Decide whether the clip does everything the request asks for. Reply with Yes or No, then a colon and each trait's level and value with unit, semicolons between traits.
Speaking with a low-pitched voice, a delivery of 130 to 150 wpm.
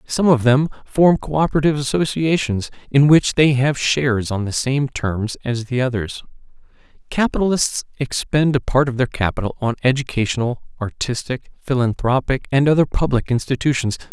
Yes: low, 130 Hz; average, 140 wpm